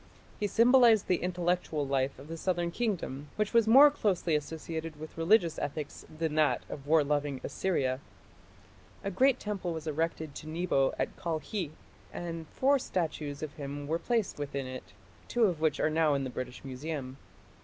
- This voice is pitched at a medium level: Yes, medium, 160 Hz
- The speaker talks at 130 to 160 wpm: No, average, 170 wpm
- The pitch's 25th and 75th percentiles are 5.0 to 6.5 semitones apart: No, average, 4.3 semitones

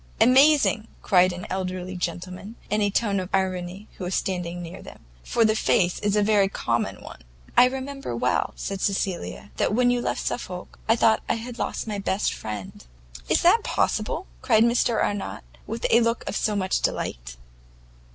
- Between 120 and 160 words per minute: No, average, 175 wpm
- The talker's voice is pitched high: Yes, high, 200 Hz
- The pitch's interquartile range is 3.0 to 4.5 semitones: Yes, average, 3.9 semitones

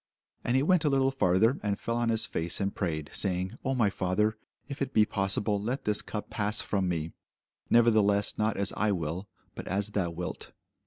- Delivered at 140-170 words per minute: No, average, 200 wpm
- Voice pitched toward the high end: No, low, 105 Hz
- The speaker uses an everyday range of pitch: Yes, average, 3.8 semitones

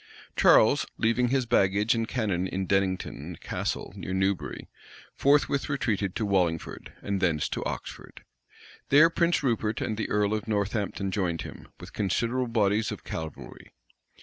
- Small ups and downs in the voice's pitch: No, average, 3.6 semitones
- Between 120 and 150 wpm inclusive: Yes, average, 145 wpm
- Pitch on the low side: Yes, low, 105 Hz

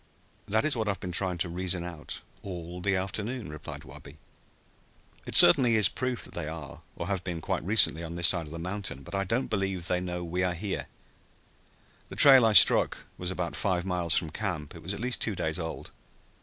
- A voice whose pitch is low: Yes, very low, 90 Hz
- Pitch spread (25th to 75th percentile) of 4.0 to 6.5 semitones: No, average, 3.1 semitones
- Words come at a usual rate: No, fast, 215 wpm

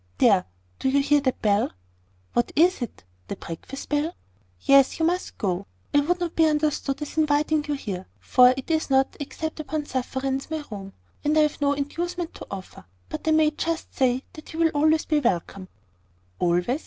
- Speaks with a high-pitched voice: Yes, very high, 290 Hz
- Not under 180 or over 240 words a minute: Yes, average, 190 wpm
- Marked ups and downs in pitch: No, average, 3.8 semitones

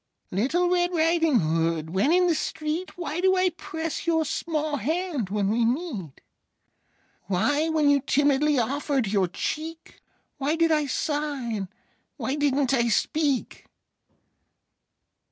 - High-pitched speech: Yes, very high, 290 Hz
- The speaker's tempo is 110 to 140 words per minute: Yes, slow, 135 wpm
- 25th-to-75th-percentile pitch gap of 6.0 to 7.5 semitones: No, wide, 5.5 semitones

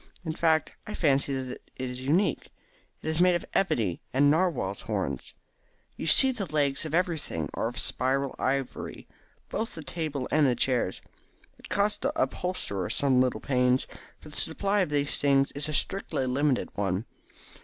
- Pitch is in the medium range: Yes, medium, 145 Hz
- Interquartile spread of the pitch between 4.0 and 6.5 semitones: Yes, average, 4.6 semitones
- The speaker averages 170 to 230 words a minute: Yes, average, 175 wpm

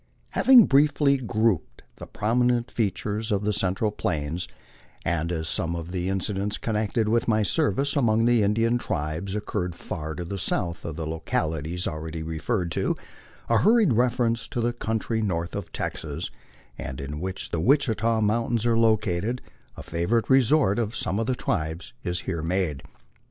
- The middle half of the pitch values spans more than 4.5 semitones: Yes, wide, 5.4 semitones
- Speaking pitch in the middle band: No, low, 105 Hz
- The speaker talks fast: No, average, 165 wpm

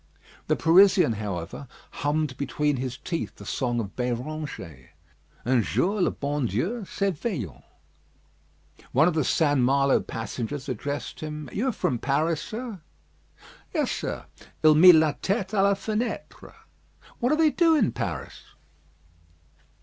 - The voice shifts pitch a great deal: Yes, wide, 7.3 semitones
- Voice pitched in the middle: Yes, medium, 150 Hz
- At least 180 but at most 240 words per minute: No, slow, 135 wpm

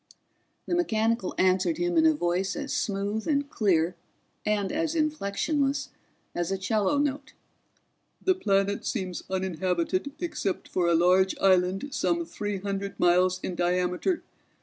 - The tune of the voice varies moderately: No, wide, 7.0 semitones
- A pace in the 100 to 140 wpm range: Yes, slow, 135 wpm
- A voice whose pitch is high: Yes, high, 195 Hz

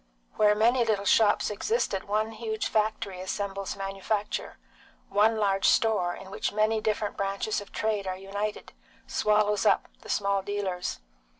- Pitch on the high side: Yes, high, 205 Hz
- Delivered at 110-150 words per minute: Yes, average, 140 wpm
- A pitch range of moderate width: No, narrow, 1.7 semitones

